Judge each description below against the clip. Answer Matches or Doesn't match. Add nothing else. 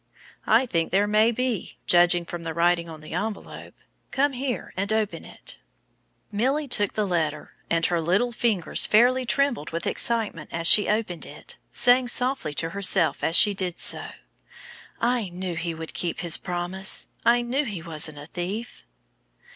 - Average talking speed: Matches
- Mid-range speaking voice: Doesn't match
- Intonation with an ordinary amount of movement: Doesn't match